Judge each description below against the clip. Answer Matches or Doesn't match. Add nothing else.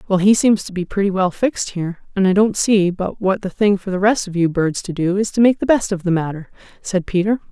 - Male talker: Doesn't match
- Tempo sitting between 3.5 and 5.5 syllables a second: Doesn't match